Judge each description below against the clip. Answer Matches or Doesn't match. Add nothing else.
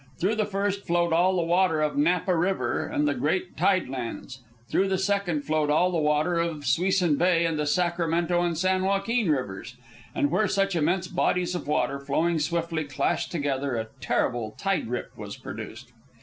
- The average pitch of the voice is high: Doesn't match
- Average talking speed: Matches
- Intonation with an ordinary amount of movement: Matches